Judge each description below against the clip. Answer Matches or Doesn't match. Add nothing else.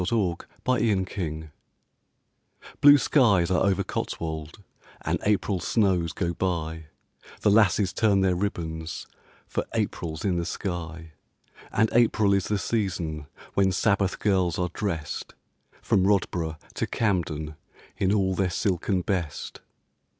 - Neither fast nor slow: Doesn't match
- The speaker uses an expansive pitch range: Doesn't match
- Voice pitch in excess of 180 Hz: Doesn't match